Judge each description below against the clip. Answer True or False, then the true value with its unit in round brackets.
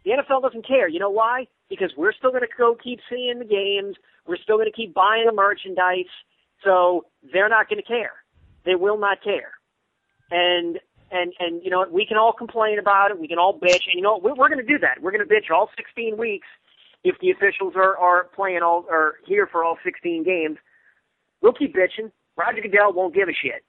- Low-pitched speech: False (200 Hz)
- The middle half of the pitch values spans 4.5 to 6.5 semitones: True (5.2 semitones)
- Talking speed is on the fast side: True (220 wpm)